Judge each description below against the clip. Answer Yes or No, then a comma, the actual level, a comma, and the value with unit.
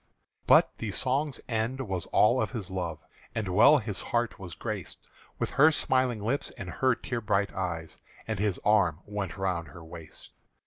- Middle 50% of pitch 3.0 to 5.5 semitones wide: Yes, average, 4.8 semitones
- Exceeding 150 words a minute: Yes, average, 175 wpm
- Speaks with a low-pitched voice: Yes, low, 105 Hz